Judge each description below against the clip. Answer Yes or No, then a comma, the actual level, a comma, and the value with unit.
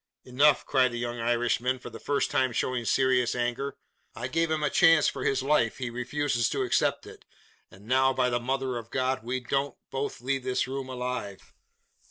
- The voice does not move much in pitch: Yes, narrow, 1.9 semitones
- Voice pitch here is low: Yes, low, 130 Hz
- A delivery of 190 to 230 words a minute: Yes, average, 195 wpm